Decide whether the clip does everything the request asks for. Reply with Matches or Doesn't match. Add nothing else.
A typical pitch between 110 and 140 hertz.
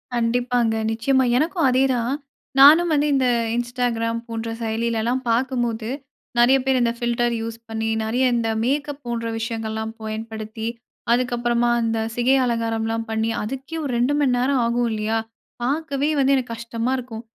Doesn't match